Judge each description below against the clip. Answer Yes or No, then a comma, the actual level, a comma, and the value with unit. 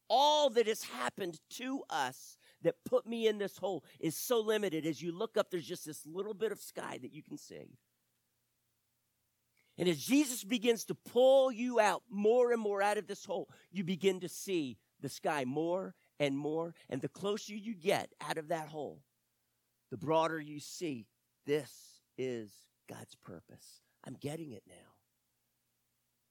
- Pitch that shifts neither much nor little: No, wide, 8.1 semitones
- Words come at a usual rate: Yes, average, 170 wpm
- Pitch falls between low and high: Yes, medium, 180 Hz